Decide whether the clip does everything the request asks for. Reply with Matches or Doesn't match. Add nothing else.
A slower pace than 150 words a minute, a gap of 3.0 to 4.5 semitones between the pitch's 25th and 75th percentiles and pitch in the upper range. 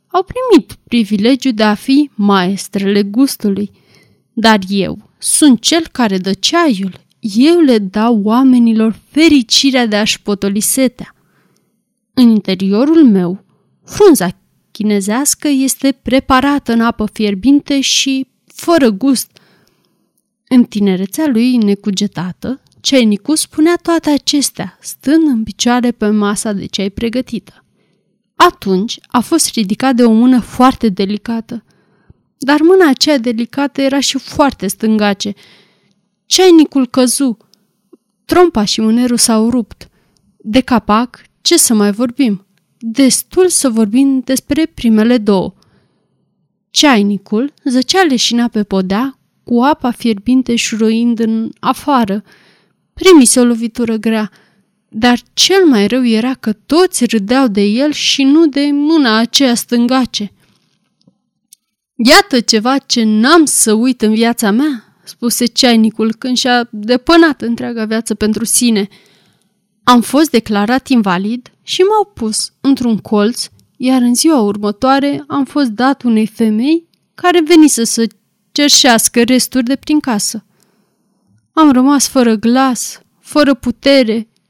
Matches